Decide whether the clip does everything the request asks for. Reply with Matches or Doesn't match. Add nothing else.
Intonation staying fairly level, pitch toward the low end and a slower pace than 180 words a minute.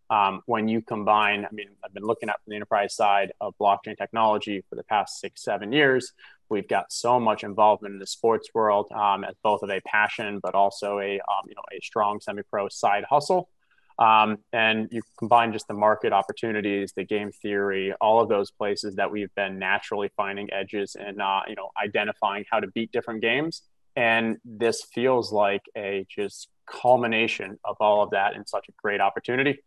Doesn't match